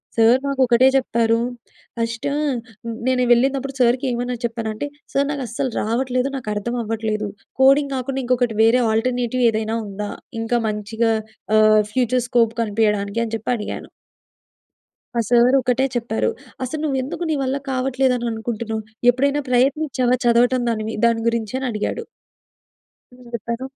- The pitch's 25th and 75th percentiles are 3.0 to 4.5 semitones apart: No, narrow, 2.5 semitones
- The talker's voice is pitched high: Yes, high, 240 Hz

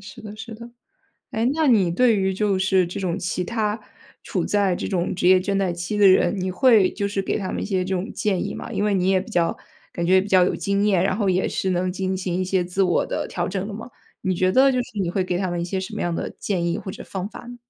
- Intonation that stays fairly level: Yes, narrow, 2.1 semitones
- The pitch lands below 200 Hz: Yes, high, 190 Hz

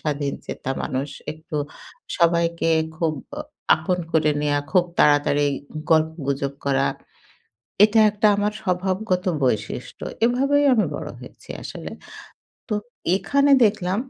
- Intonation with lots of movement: Yes, wide, 5.9 semitones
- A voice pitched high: No, medium, 170 Hz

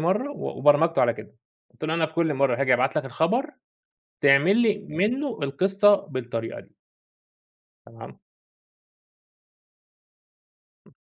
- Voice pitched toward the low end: No, medium, 155 Hz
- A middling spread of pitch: No, wide, 7.0 semitones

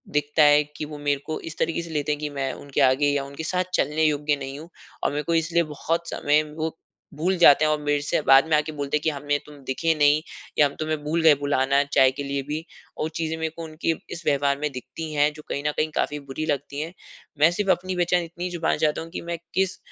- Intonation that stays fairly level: Yes, narrow, 2.0 semitones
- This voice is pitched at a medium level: Yes, medium, 150 Hz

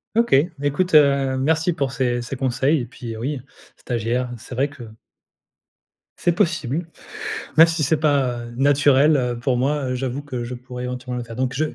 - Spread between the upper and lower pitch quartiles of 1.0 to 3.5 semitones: Yes, average, 2.9 semitones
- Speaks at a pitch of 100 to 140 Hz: Yes, low, 135 Hz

